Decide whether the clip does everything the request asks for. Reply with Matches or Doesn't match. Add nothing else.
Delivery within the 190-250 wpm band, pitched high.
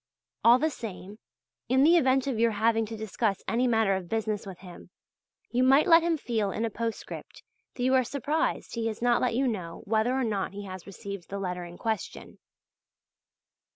Matches